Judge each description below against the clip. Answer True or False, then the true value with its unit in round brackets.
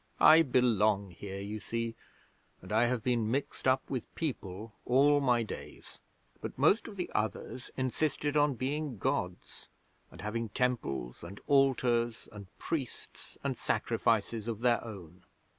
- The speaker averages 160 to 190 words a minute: False (140 wpm)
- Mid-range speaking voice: False (115 Hz)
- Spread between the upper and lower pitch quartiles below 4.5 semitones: True (4.0 semitones)